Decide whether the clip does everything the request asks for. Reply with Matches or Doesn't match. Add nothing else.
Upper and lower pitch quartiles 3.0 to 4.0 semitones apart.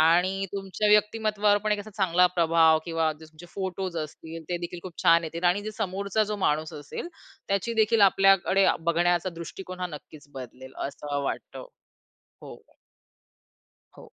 Matches